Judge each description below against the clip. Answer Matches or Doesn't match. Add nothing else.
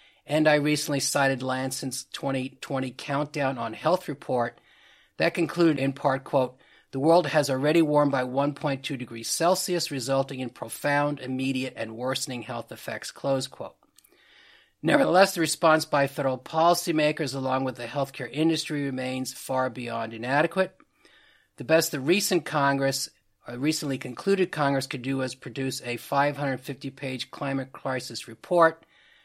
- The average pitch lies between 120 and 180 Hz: Matches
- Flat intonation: Doesn't match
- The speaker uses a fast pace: Doesn't match